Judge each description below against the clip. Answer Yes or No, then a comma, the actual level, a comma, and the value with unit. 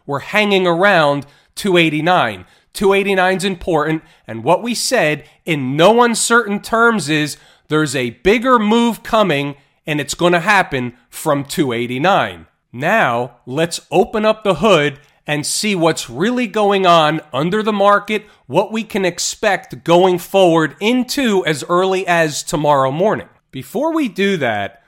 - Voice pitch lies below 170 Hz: No, medium, 175 Hz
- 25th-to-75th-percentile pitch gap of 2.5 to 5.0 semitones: No, wide, 5.4 semitones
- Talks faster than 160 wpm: No, average, 140 wpm